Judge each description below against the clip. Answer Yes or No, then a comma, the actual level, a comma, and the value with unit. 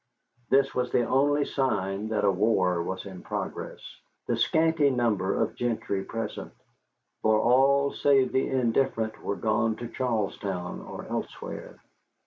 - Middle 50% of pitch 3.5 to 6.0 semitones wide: Yes, average, 4.8 semitones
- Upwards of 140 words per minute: No, slow, 135 wpm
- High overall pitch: No, low, 115 Hz